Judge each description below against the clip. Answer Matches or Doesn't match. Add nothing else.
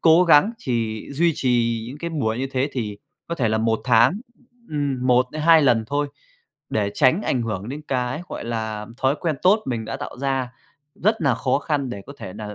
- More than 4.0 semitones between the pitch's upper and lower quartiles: Matches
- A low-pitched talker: Matches